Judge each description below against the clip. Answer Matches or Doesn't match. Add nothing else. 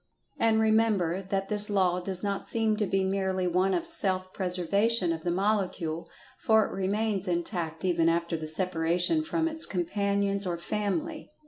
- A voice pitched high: Matches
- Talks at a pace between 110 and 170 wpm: Matches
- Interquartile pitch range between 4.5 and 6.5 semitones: Doesn't match